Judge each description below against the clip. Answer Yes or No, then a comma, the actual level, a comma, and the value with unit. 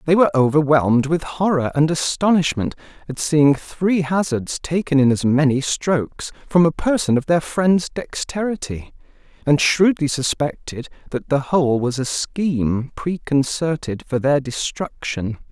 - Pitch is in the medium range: Yes, medium, 150 Hz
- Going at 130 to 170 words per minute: Yes, average, 140 wpm